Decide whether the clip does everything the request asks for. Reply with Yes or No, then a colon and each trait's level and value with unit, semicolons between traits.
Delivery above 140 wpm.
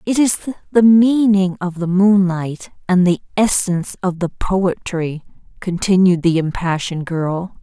No: slow, 135 wpm